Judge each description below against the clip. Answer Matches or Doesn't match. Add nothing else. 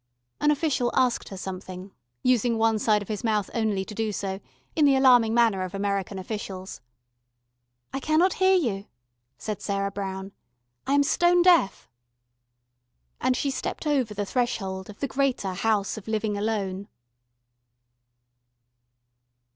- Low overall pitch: Doesn't match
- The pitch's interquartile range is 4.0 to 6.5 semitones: Matches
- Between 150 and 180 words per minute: Doesn't match